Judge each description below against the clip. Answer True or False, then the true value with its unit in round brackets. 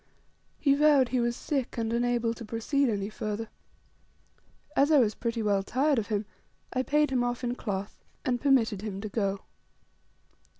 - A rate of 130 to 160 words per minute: False (170 wpm)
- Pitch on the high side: True (235 Hz)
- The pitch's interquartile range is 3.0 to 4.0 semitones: True (3.6 semitones)